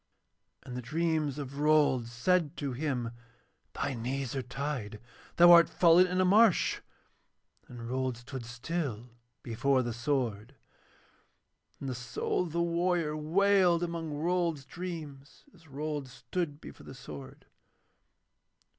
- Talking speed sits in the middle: No, slow, 130 wpm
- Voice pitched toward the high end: No, medium, 145 Hz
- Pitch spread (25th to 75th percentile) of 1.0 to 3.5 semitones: No, average, 5.1 semitones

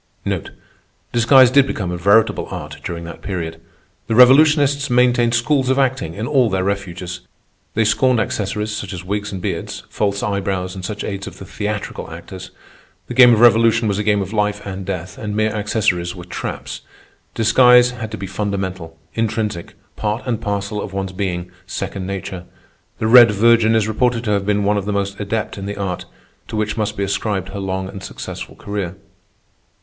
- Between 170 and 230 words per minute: Yes, average, 185 wpm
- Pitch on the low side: Yes, low, 105 Hz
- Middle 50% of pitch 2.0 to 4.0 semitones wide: Yes, average, 2.8 semitones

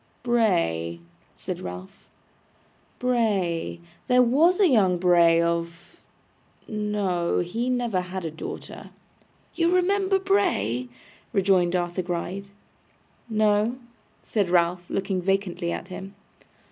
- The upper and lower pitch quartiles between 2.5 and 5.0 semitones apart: No, wide, 5.4 semitones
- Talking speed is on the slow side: Yes, slow, 100 wpm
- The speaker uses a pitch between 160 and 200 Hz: Yes, high, 190 Hz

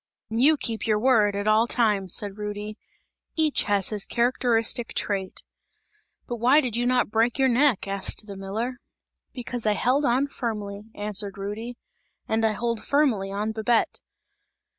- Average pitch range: Yes, average, 3.0 semitones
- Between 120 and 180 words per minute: Yes, average, 160 wpm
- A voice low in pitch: No, high, 225 Hz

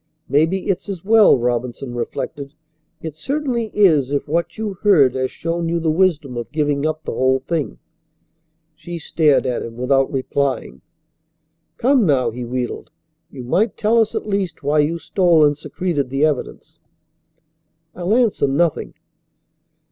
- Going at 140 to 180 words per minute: Yes, average, 150 wpm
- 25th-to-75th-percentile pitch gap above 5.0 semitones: Yes, wide, 5.4 semitones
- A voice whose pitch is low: No, medium, 155 Hz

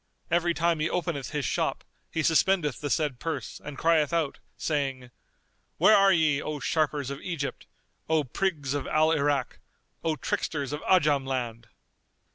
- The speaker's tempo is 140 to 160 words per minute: Yes, average, 155 wpm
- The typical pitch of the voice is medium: Yes, medium, 150 Hz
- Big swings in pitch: No, average, 2.8 semitones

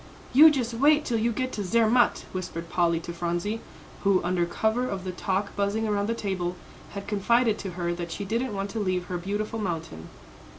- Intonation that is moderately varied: Yes, average, 4.2 semitones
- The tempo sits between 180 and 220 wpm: Yes, average, 200 wpm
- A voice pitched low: No, high, 200 Hz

